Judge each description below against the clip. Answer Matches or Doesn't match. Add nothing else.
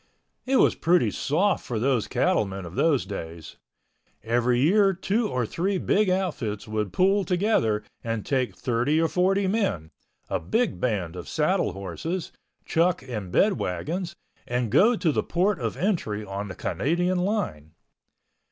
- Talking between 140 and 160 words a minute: Matches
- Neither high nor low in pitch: Matches